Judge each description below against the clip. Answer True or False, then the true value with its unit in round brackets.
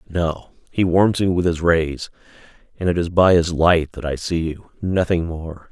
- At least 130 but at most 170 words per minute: False (190 wpm)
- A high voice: False (85 Hz)